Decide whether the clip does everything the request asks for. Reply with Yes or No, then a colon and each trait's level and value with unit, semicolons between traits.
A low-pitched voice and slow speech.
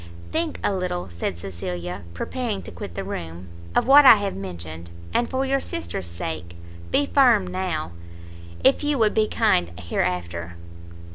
No: very low, 95 Hz; average, 155 wpm